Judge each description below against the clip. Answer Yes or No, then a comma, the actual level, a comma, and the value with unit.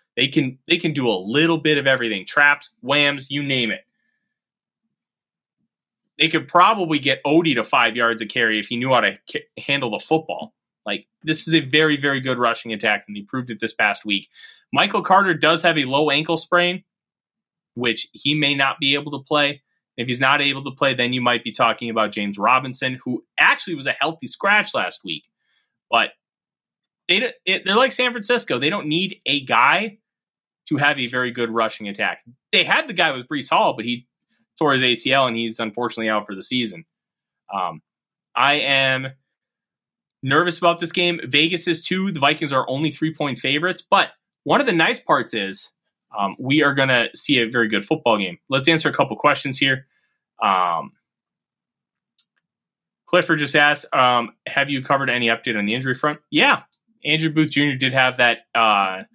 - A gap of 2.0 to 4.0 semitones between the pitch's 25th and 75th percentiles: No, average, 4.5 semitones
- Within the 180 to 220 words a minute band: Yes, average, 190 wpm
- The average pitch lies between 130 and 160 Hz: Yes, medium, 140 Hz